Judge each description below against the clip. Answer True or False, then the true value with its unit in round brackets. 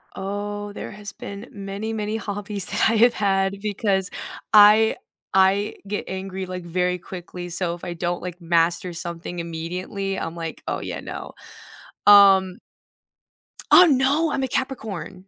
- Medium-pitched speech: False (195 Hz)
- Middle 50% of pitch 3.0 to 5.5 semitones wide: False (2.5 semitones)